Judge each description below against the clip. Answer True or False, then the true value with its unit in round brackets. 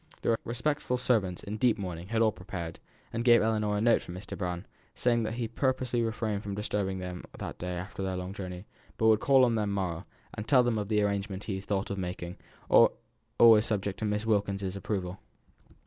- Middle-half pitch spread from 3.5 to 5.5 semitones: False (3.1 semitones)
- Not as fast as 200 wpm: False (205 wpm)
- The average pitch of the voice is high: False (105 Hz)